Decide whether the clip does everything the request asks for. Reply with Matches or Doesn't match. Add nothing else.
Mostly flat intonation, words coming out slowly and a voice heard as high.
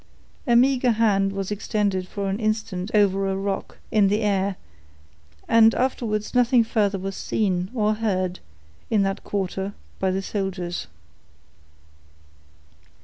Matches